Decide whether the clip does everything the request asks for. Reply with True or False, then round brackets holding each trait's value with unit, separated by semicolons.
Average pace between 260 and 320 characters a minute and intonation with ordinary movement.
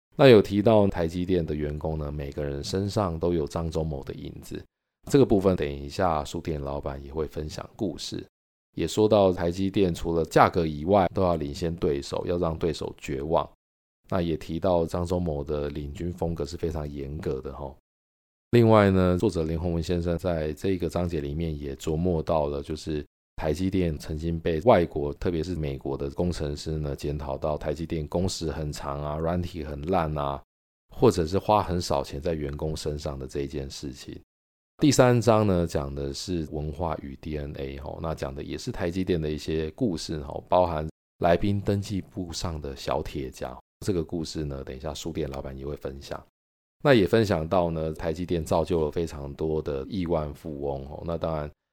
True (275 characters per minute; 3.5 semitones)